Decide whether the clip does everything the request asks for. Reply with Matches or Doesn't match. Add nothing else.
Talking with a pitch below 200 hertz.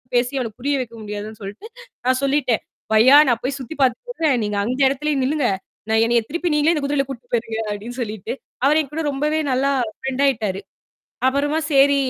Doesn't match